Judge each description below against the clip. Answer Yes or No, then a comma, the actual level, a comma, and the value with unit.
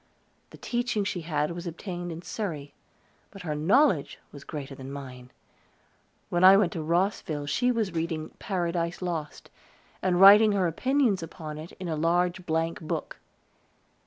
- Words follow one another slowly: No, average, 155 wpm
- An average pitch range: Yes, average, 3.6 semitones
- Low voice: No, medium, 170 Hz